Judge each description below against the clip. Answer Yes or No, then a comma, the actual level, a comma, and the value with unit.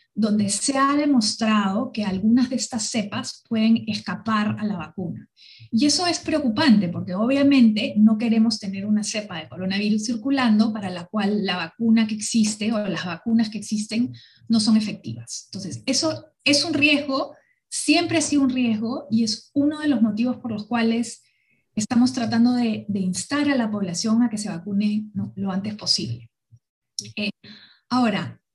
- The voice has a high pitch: Yes, high, 220 Hz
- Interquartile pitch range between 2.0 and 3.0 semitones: No, average, 3.5 semitones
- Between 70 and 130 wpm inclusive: No, average, 165 wpm